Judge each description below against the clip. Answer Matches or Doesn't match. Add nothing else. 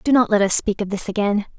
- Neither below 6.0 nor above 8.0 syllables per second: Matches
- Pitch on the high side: Matches